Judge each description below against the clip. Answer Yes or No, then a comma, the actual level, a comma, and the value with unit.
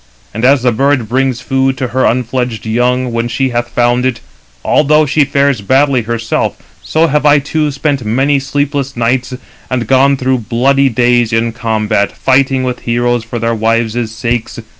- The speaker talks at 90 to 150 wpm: No, average, 170 wpm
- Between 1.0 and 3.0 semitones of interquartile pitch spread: Yes, average, 2.7 semitones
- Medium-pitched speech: No, low, 125 Hz